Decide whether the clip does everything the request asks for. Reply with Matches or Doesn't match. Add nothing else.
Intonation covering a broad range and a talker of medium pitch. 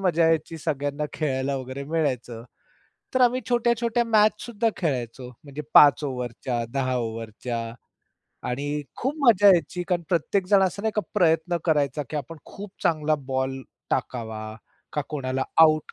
Matches